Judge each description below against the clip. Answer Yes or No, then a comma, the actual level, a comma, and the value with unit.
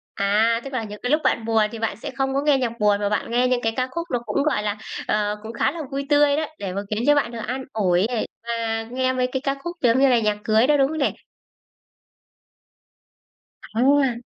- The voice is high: Yes, high, 240 Hz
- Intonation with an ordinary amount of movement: Yes, average, 3.8 semitones